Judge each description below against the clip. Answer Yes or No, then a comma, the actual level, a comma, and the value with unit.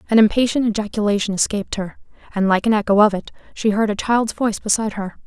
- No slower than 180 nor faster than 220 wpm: Yes, fast, 205 wpm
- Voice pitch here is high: Yes, high, 210 Hz